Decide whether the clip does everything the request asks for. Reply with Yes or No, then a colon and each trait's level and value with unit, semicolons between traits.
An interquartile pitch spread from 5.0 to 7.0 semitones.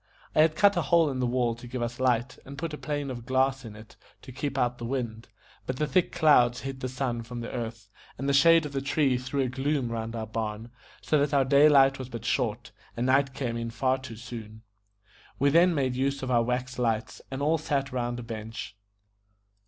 No: average, 2.9 semitones